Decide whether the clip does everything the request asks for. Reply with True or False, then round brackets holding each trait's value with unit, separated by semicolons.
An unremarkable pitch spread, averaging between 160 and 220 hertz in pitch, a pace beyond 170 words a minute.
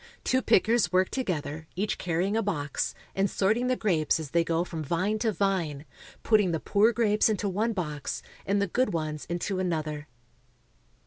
True (4.7 semitones; 185 Hz; 180 wpm)